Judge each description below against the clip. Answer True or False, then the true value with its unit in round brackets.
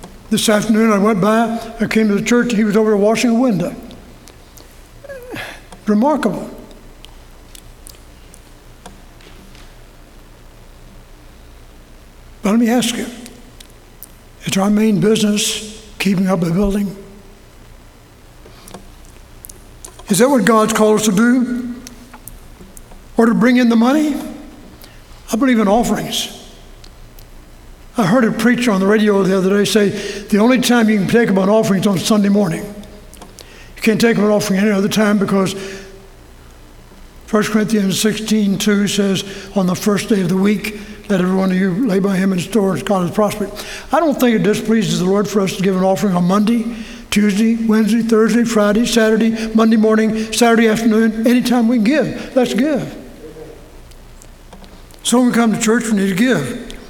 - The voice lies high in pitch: True (210 Hz)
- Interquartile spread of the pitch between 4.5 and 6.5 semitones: False (3.2 semitones)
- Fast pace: False (155 wpm)